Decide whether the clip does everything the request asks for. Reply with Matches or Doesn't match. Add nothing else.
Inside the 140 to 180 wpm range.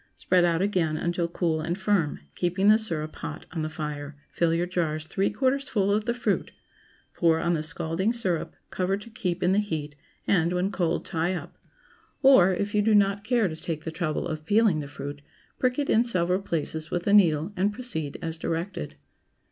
Doesn't match